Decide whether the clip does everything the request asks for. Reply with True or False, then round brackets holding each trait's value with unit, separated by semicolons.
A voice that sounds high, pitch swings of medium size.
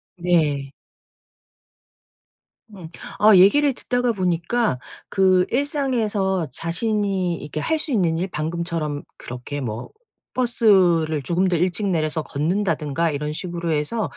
False (175 Hz; 5.0 semitones)